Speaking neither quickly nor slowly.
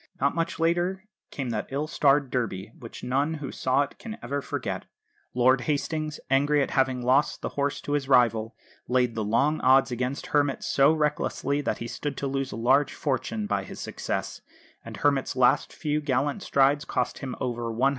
Yes: average, 185 wpm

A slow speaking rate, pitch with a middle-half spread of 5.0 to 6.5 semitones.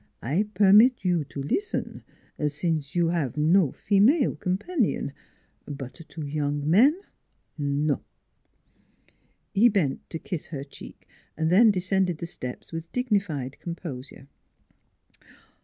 Yes: slow, 120 wpm; wide, 5.4 semitones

